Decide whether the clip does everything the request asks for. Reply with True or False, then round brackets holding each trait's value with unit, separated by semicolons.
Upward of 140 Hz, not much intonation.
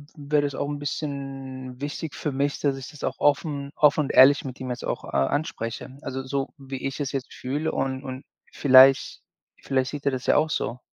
False (135 Hz; 1.7 semitones)